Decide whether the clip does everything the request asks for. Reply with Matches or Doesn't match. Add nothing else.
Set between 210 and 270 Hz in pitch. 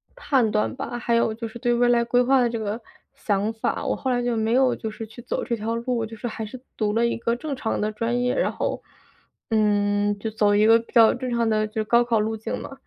Matches